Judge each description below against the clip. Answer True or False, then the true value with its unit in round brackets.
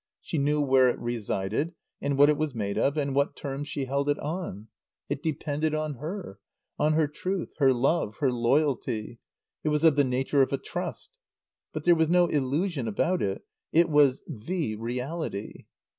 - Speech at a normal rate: True (180 wpm)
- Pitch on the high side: False (145 Hz)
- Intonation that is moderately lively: True (3.6 semitones)